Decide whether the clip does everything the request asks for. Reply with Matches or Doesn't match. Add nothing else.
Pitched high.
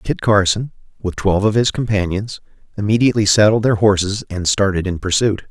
Doesn't match